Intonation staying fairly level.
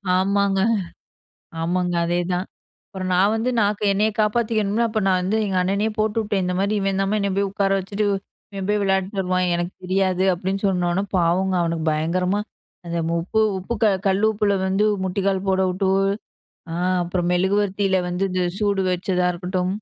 Yes: narrow, 1.9 semitones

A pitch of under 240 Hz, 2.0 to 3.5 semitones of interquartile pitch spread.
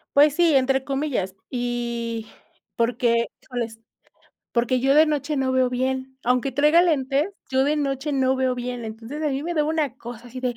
No: very high, 260 Hz; average, 2.8 semitones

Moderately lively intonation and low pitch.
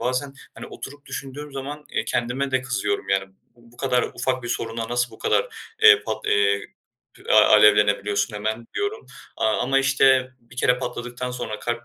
Yes: average, 3.2 semitones; low, 125 Hz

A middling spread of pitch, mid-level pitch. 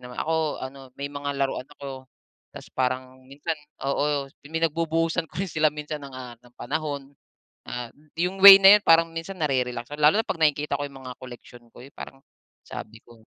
Yes: average, 3.7 semitones; medium, 145 Hz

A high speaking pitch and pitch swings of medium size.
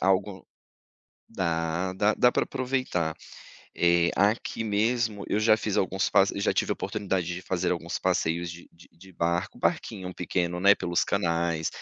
No: very low, 95 Hz; average, 3.1 semitones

